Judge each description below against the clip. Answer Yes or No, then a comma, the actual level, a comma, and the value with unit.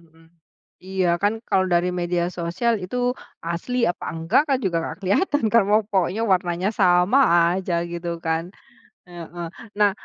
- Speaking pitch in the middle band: Yes, medium, 180 Hz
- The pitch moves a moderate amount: Yes, average, 3.3 semitones